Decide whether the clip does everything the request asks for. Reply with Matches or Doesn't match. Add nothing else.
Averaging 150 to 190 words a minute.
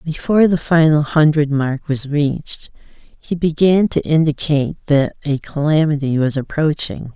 Doesn't match